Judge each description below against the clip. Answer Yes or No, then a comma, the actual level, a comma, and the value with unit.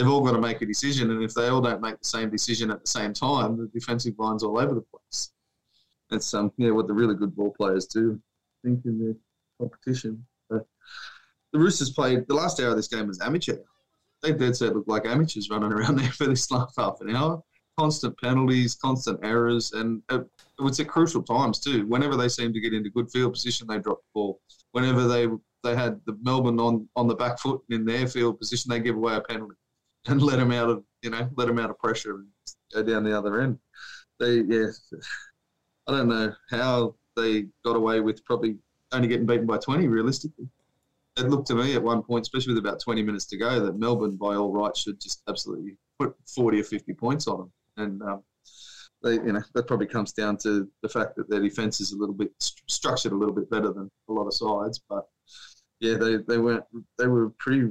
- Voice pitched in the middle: No, low, 115 Hz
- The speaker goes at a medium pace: No, fast, 225 wpm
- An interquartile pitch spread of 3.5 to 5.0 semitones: No, narrow, 2.4 semitones